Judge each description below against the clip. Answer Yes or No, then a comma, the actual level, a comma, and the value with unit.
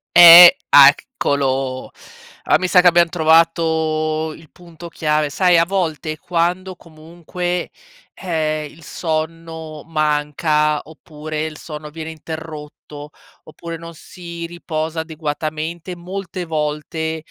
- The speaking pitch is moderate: Yes, medium, 160 Hz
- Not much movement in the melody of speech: Yes, narrow, 1.8 semitones